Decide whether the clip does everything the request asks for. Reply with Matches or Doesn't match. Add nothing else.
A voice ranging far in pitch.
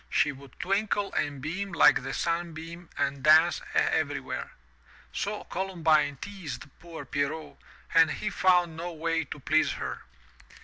Doesn't match